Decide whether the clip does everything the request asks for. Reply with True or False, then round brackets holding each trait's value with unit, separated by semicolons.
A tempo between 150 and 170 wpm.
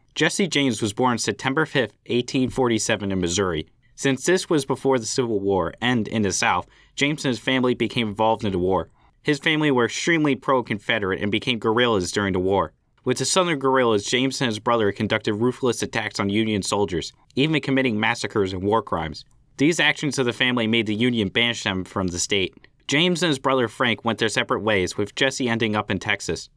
False (200 wpm)